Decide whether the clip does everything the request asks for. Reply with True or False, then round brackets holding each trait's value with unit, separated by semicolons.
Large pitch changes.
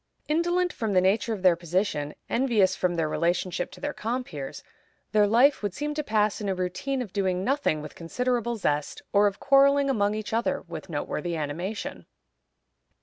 True (5.8 semitones)